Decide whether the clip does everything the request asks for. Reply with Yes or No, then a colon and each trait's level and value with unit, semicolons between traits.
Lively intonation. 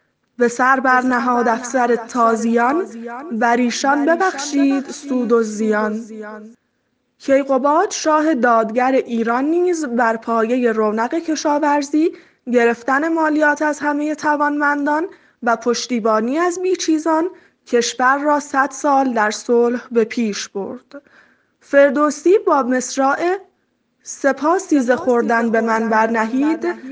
No: average, 4.2 semitones